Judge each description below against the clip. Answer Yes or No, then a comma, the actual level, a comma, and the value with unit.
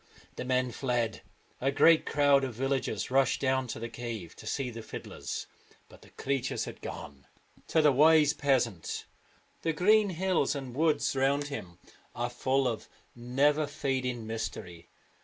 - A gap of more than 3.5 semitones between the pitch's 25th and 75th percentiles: No, average, 3.2 semitones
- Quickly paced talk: No, average, 155 wpm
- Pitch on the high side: No, low, 130 Hz